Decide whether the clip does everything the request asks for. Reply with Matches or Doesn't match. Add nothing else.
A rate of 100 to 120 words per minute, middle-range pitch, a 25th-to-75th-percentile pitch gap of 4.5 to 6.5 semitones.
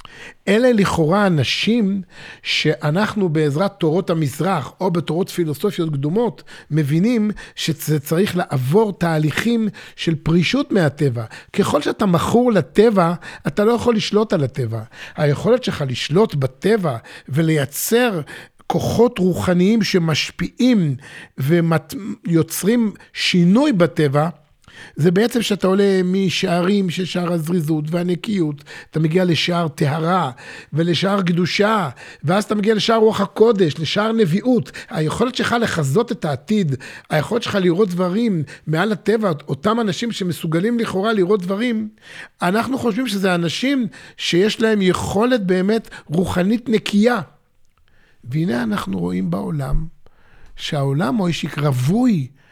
Matches